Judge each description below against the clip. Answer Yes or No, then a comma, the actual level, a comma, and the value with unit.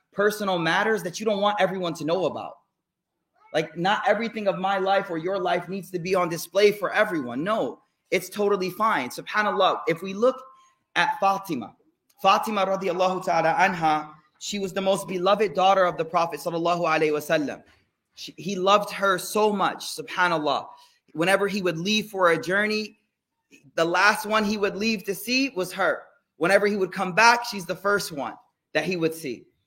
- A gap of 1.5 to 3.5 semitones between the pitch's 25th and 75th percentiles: Yes, average, 2.8 semitones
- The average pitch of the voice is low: No, high, 195 Hz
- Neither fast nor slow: Yes, average, 180 wpm